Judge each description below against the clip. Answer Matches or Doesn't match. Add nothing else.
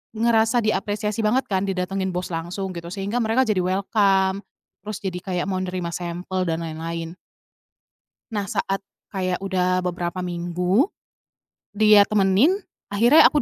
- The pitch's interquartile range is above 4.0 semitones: Doesn't match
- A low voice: Doesn't match